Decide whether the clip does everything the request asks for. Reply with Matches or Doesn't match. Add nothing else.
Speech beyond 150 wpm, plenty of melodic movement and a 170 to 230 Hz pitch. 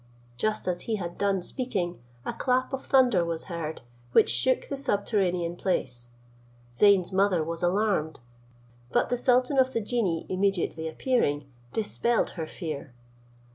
Doesn't match